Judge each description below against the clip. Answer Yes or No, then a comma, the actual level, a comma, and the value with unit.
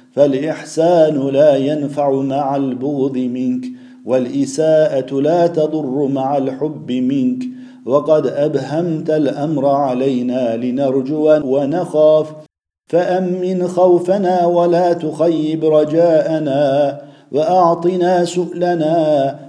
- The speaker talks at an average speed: No, slow, 75 wpm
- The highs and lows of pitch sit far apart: No, average, 3.8 semitones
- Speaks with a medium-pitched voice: Yes, medium, 155 Hz